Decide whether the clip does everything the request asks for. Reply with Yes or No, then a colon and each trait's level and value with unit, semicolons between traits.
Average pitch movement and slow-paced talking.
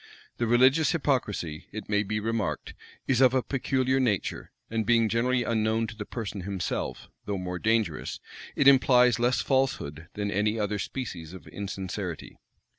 No: average, 3.8 semitones; average, 155 wpm